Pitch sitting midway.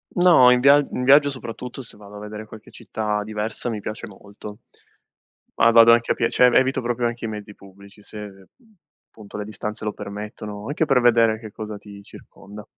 No: low, 110 Hz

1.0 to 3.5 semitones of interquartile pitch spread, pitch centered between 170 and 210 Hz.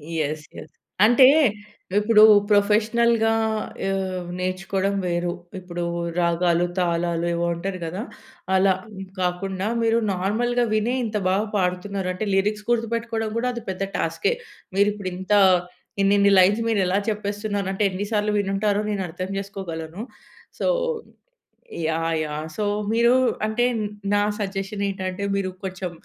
Yes: narrow, 2.6 semitones; high, 195 Hz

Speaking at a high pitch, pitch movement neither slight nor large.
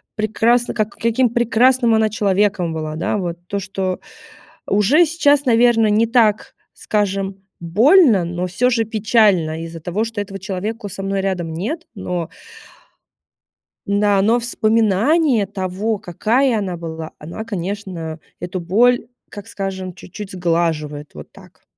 Yes: high, 205 Hz; average, 4.1 semitones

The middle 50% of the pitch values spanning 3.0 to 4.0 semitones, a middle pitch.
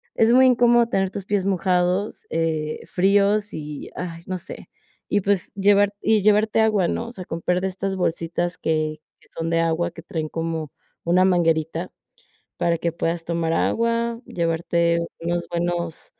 Yes: average, 3.4 semitones; medium, 175 Hz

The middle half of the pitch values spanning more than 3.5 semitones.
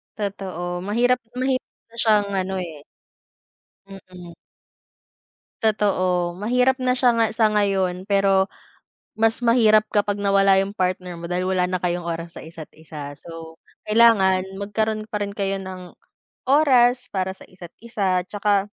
No: average, 3.1 semitones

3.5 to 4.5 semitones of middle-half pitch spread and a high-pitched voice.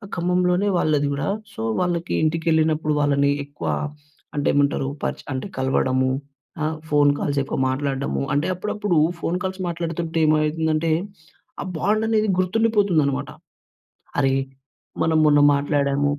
No: average, 3.9 semitones; medium, 155 Hz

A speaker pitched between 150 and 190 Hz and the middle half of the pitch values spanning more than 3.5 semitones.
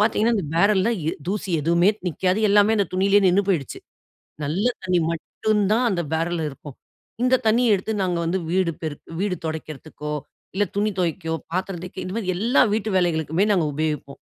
Yes: medium, 185 Hz; average, 3.9 semitones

